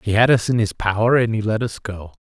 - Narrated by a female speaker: No, male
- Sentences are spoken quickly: Yes, fast, 295 wpm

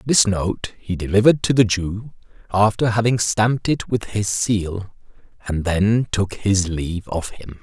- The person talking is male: Yes, male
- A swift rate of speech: No, average, 165 wpm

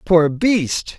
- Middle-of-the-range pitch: Yes, medium, 175 Hz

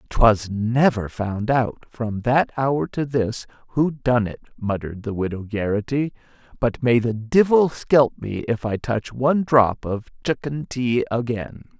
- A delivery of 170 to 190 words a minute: No, average, 160 wpm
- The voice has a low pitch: Yes, low, 120 Hz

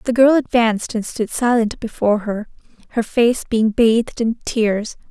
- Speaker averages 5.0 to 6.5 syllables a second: No, 4.7 syllables/s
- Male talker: No, female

